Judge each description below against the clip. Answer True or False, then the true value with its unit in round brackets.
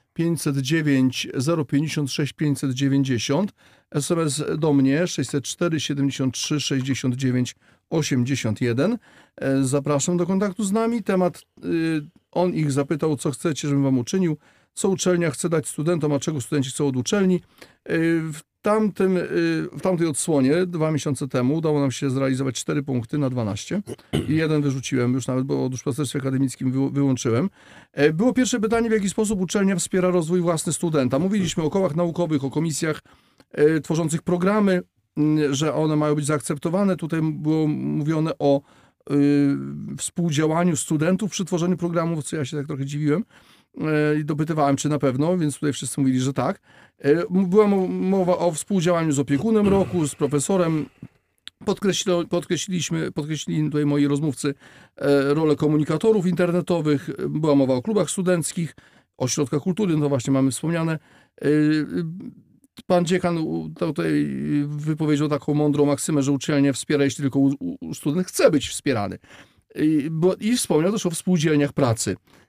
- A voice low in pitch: False (155 Hz)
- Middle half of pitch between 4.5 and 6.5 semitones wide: False (3.8 semitones)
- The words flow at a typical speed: True (135 wpm)